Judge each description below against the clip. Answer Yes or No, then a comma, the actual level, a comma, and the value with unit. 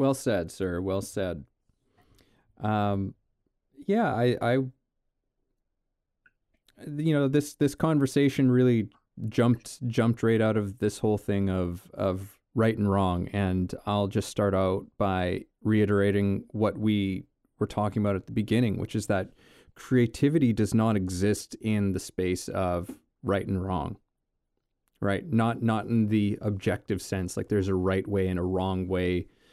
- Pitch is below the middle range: Yes, low, 105 Hz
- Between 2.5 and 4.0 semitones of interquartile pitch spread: Yes, average, 3.5 semitones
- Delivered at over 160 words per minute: No, average, 150 wpm